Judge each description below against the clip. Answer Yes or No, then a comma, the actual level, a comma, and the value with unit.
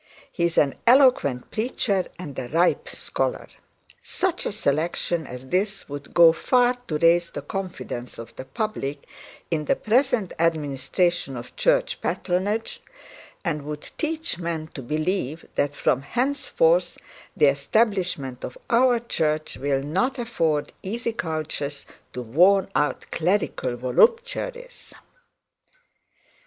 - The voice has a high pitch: No, medium, 170 Hz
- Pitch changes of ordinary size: No, wide, 8.0 semitones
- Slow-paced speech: Yes, slow, 125 wpm